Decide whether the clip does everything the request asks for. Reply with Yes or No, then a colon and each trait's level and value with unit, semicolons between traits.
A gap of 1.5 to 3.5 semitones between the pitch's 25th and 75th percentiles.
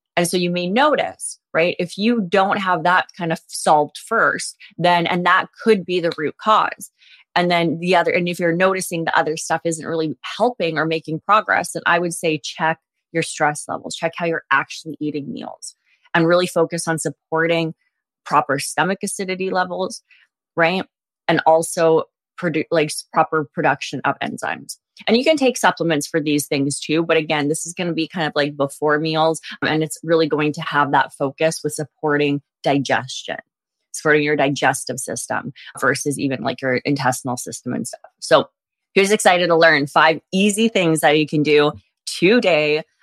Yes: average, 3.1 semitones